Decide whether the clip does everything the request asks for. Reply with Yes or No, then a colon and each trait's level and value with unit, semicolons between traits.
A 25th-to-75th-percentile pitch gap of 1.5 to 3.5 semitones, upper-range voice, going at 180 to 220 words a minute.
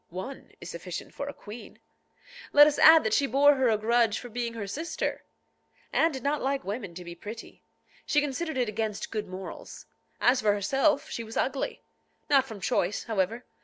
No: average, 5.0 semitones; high, 235 Hz; average, 190 wpm